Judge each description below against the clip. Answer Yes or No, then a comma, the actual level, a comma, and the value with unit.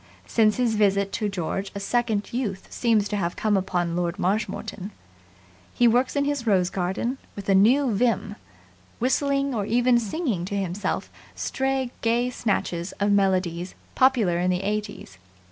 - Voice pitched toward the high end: Yes, high, 210 Hz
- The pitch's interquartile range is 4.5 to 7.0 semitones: No, average, 4.1 semitones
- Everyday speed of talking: Yes, average, 155 wpm